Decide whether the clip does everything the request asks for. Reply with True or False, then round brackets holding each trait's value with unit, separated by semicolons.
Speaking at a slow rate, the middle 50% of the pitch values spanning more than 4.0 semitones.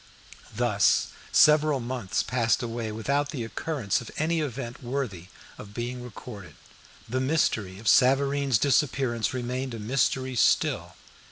False (125 wpm; 3.3 semitones)